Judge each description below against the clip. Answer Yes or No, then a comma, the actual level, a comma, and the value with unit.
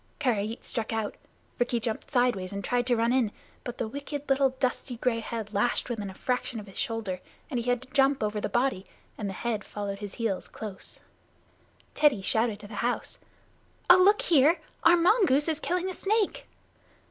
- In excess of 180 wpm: Yes, average, 190 wpm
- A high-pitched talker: Yes, high, 240 Hz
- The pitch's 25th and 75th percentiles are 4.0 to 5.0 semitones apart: Yes, average, 4.4 semitones